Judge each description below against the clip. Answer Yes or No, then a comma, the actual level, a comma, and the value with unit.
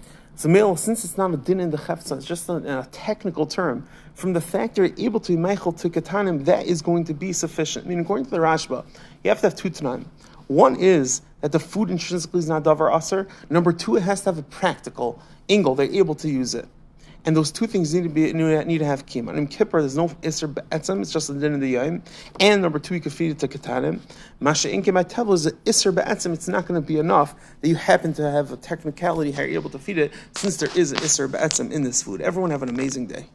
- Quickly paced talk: Yes, fast, 250 wpm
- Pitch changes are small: No, average, 3.5 semitones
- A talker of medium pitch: Yes, medium, 165 Hz